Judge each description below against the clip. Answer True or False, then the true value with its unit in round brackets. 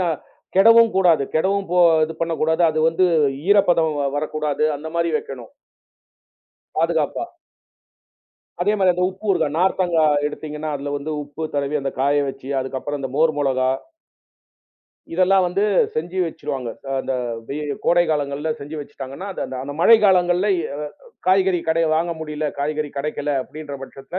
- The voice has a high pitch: False (155 Hz)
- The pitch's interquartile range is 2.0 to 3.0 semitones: False (3.9 semitones)